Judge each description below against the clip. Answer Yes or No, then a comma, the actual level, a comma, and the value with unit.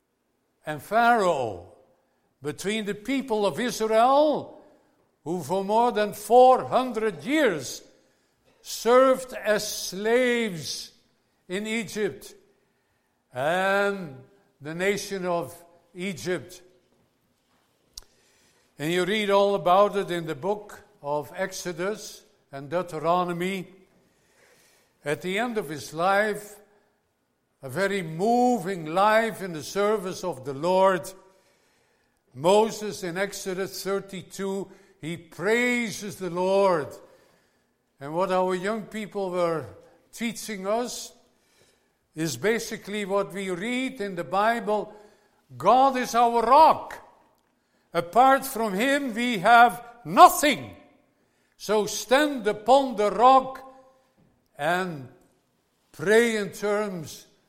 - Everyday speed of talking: No, slow, 100 wpm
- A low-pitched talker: No, high, 200 Hz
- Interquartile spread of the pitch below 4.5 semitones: Yes, average, 4.0 semitones